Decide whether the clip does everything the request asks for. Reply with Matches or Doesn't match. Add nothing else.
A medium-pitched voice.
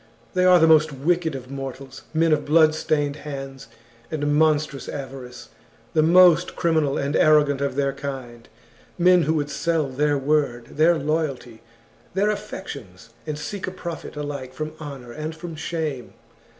Matches